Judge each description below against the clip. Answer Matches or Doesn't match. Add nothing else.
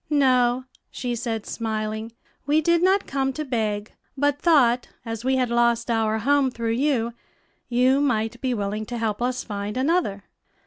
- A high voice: Matches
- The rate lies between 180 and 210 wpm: Doesn't match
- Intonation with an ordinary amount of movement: Matches